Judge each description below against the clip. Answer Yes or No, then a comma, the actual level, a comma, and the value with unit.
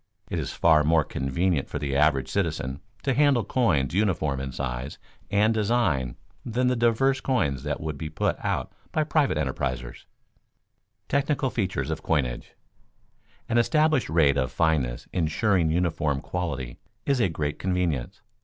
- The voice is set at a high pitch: No, very low, 80 Hz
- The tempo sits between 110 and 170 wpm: Yes, average, 150 wpm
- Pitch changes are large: Yes, wide, 8.9 semitones